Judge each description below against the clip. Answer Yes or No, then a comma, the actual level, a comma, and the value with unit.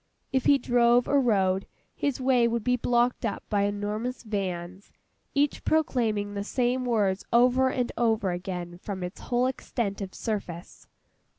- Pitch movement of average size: Yes, average, 4.0 semitones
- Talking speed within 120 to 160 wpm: Yes, average, 155 wpm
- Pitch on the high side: Yes, high, 225 Hz